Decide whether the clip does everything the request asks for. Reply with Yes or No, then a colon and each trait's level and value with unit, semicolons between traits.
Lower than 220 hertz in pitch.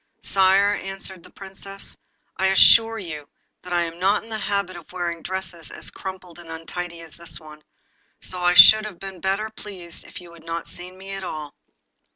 Yes: medium, 185 Hz